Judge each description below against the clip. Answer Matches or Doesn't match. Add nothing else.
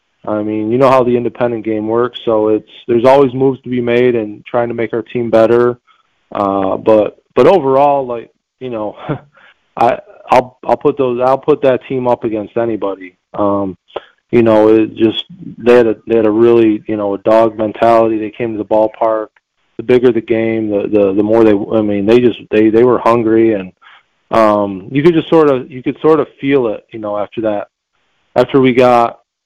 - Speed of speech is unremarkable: Doesn't match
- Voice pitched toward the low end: Matches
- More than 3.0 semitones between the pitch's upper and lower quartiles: Doesn't match